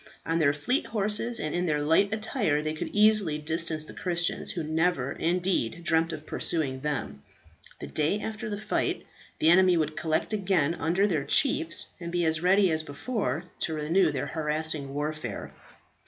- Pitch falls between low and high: Yes, medium, 165 Hz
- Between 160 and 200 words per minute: Yes, average, 170 wpm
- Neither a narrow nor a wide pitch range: Yes, average, 3.8 semitones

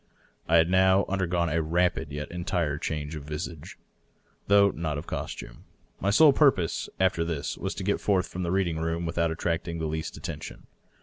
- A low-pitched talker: Yes, very low, 85 Hz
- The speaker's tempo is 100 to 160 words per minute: No, average, 190 wpm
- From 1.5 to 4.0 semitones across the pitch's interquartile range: Yes, average, 2.8 semitones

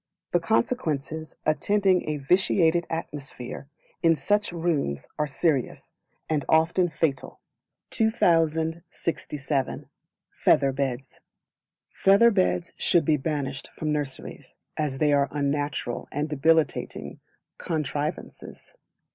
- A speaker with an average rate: No, slow, 95 wpm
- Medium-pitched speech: Yes, medium, 155 Hz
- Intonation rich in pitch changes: No, average, 3.2 semitones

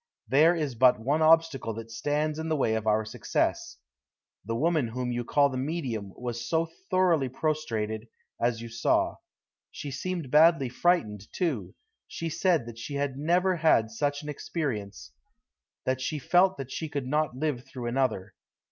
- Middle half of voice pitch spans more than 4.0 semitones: Yes, average, 5.3 semitones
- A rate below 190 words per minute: Yes, average, 165 wpm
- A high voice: No, low, 135 Hz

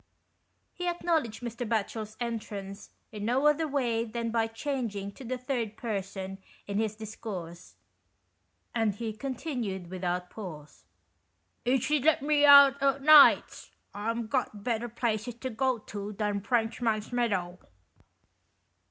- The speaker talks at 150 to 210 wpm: No, average, 140 wpm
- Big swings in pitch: No, average, 3.9 semitones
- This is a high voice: Yes, high, 225 Hz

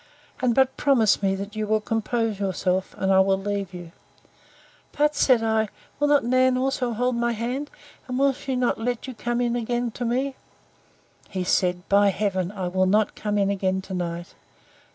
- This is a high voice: Yes, high, 220 Hz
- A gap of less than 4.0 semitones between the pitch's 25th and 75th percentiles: No, average, 4.4 semitones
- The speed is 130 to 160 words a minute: No, average, 185 wpm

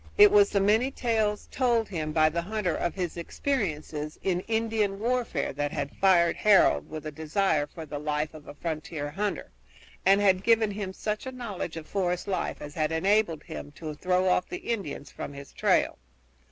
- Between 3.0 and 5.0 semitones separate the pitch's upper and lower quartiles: No, wide, 5.5 semitones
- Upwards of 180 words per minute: Yes, average, 190 wpm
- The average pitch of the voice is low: No, medium, 185 Hz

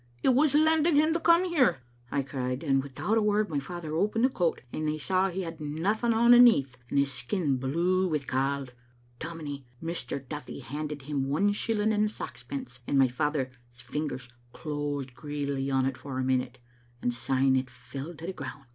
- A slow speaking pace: No, average, 190 wpm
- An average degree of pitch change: No, wide, 6.2 semitones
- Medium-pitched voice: Yes, medium, 150 Hz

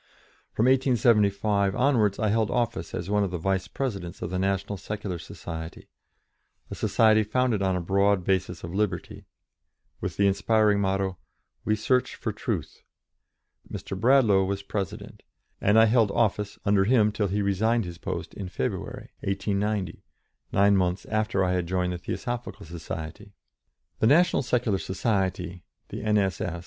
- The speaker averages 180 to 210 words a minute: No, average, 140 wpm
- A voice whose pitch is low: Yes, low, 100 Hz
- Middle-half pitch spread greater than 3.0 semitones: No, narrow, 2.6 semitones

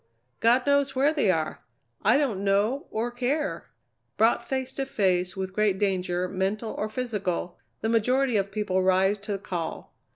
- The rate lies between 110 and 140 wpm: No, average, 165 wpm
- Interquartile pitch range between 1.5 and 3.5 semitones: No, average, 4.9 semitones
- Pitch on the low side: No, high, 210 Hz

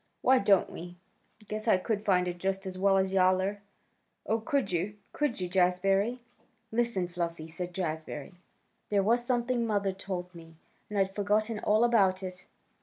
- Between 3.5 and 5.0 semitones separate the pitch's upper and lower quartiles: No, average, 3.0 semitones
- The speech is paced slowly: No, average, 165 wpm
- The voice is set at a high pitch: Yes, high, 195 Hz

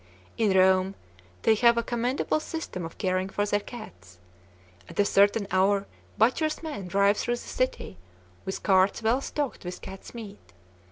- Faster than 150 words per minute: Yes, average, 160 wpm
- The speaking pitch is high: Yes, high, 205 Hz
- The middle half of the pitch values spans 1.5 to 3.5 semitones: No, average, 3.9 semitones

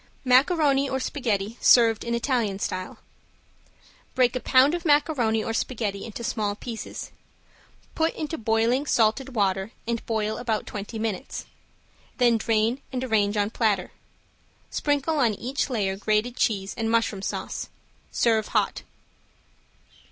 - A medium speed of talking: No, slow, 130 wpm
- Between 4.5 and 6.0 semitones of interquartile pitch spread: No, average, 3.4 semitones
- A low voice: No, high, 230 Hz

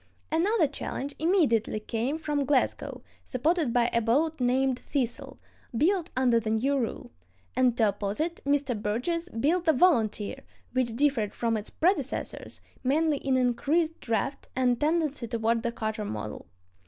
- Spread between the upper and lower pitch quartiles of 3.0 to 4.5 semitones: No, average, 5.1 semitones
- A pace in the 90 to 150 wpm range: Yes, average, 145 wpm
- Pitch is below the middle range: No, very high, 260 Hz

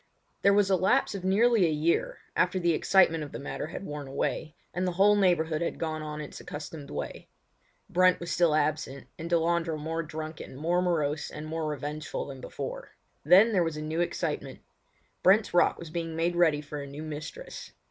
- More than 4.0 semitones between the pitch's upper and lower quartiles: No, average, 3.0 semitones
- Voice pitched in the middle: Yes, medium, 165 Hz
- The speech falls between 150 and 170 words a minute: No, average, 195 wpm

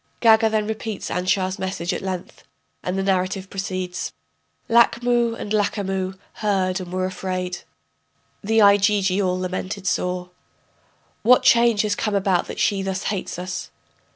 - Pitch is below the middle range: No, high, 195 Hz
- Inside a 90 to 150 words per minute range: Yes, average, 140 wpm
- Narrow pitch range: Yes, narrow, 2.3 semitones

